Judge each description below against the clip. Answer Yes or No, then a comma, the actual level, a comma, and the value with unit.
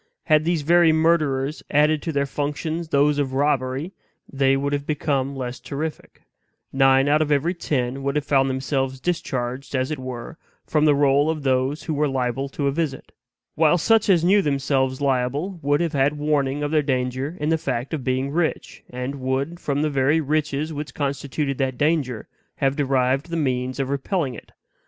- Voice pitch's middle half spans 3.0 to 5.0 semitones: No, narrow, 2.5 semitones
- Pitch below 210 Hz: Yes, medium, 140 Hz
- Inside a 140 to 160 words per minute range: No, average, 185 wpm